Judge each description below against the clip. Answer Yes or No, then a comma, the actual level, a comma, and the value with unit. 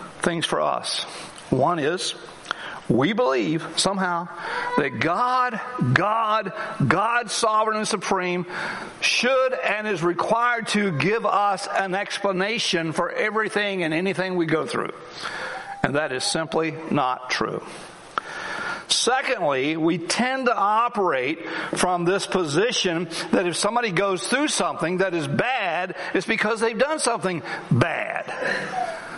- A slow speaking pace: Yes, slow, 125 wpm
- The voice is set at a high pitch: Yes, high, 195 Hz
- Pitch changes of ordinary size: Yes, average, 4.7 semitones